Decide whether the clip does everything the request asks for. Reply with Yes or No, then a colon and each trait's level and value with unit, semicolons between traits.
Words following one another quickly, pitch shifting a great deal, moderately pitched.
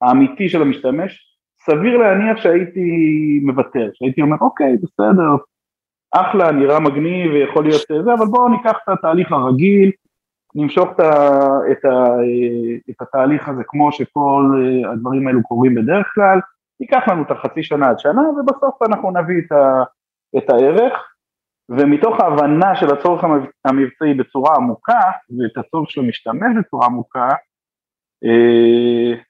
No: average, 130 wpm; wide, 6.0 semitones; medium, 145 Hz